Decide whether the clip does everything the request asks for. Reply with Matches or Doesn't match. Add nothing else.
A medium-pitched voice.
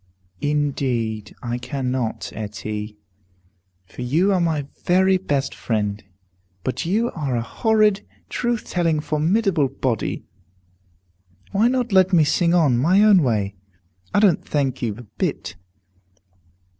Matches